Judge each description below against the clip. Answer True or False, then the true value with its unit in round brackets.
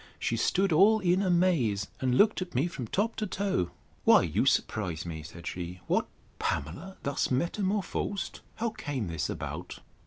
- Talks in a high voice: False (165 Hz)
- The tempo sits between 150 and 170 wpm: True (160 wpm)